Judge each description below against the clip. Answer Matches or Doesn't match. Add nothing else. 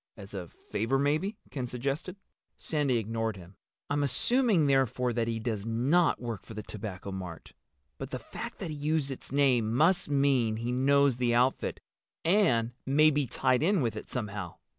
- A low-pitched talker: Matches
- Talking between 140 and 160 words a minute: Doesn't match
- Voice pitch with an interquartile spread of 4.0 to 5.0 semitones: Matches